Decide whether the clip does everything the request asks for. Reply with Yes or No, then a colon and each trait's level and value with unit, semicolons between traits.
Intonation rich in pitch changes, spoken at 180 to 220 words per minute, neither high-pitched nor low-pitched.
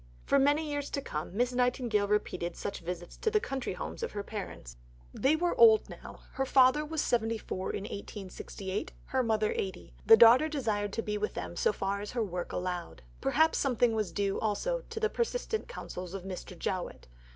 No: wide, 6.5 semitones; average, 190 wpm; high, 225 Hz